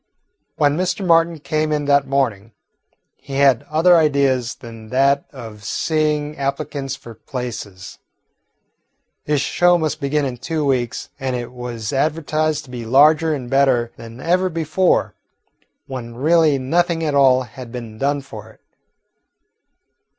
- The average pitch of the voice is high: No, medium, 140 Hz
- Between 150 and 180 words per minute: No, average, 140 wpm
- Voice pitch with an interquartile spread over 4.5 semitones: No, average, 3.9 semitones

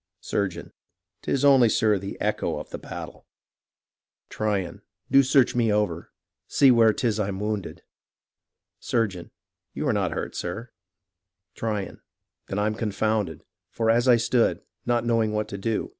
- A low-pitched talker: Yes, low, 110 Hz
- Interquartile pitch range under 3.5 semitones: Yes, average, 2.7 semitones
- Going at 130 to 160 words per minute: Yes, average, 145 wpm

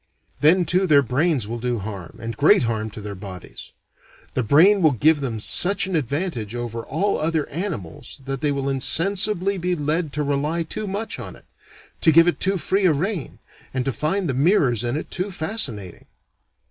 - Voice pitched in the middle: Yes, medium, 150 Hz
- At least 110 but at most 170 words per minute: No, average, 190 wpm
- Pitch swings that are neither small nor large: No, wide, 6.9 semitones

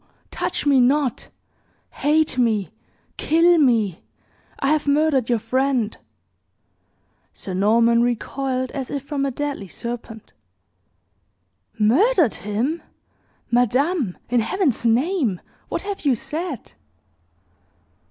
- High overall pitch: Yes, very high, 260 Hz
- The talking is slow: Yes, slow, 105 wpm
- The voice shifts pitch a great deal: No, average, 4.5 semitones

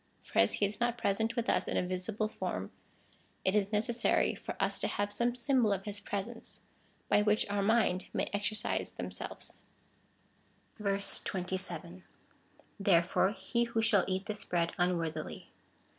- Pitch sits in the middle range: No, high, 205 Hz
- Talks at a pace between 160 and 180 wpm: No, average, 150 wpm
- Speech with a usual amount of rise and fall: Yes, average, 3.0 semitones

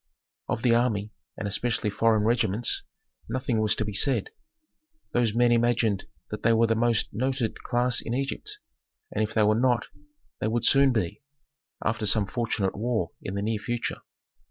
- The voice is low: Yes, low, 115 Hz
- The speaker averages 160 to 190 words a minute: Yes, average, 170 wpm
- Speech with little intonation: Yes, narrow, 2.2 semitones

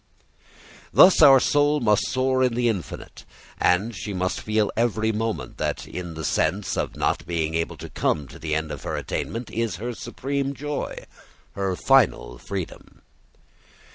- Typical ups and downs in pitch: No, wide, 6.4 semitones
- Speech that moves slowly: No, average, 160 wpm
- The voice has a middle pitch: No, low, 110 Hz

